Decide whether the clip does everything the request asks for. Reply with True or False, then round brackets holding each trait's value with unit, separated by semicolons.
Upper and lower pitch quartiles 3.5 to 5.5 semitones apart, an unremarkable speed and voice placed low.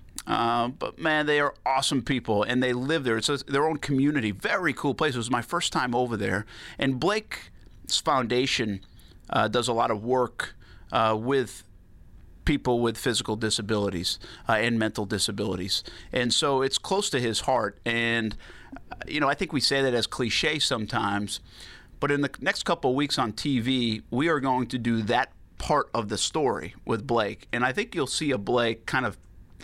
True (4.0 semitones; 190 wpm; 120 Hz)